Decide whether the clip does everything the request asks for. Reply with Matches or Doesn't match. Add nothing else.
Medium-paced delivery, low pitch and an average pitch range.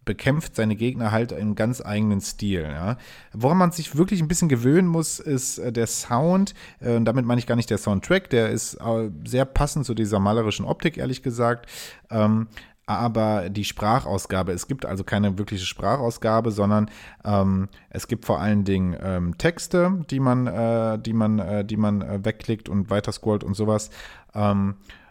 Matches